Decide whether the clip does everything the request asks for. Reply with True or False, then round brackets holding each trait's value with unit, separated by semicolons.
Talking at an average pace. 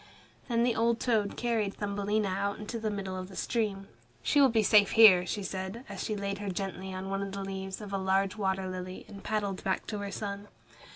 False (225 wpm)